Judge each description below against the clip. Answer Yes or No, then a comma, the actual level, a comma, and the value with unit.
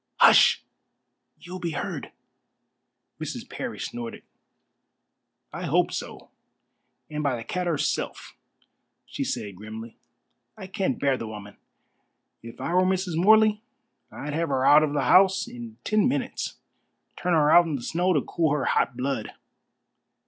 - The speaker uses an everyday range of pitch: No, wide, 6.8 semitones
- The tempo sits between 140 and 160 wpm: Yes, average, 150 wpm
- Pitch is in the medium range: Yes, medium, 150 Hz